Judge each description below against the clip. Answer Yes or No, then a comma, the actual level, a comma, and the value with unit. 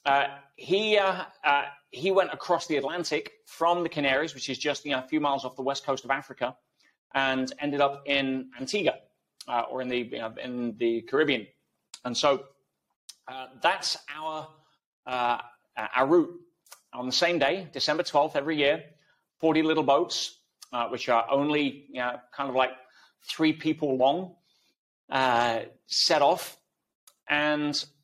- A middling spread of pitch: Yes, average, 3.1 semitones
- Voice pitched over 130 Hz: Yes, medium, 140 Hz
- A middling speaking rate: Yes, average, 160 wpm